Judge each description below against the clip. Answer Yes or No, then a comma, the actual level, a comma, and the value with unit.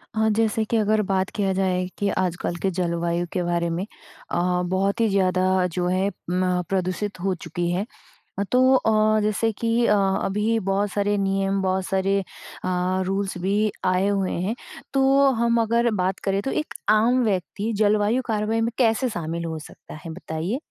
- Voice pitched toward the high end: Yes, high, 195 Hz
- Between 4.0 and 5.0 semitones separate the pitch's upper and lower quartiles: No, average, 2.9 semitones